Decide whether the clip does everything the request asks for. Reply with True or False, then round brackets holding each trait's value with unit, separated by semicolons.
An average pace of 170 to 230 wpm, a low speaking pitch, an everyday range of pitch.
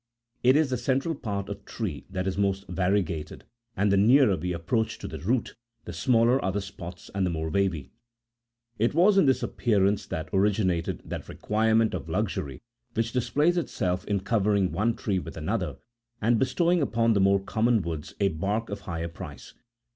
True (180 wpm; 100 Hz; 4.1 semitones)